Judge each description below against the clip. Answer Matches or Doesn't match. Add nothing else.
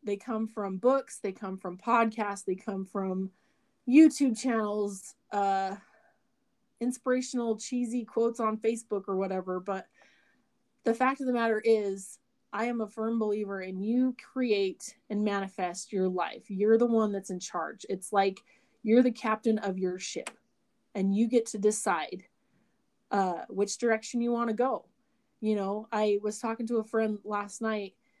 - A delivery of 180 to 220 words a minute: Doesn't match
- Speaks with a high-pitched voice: Matches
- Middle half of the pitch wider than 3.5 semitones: Doesn't match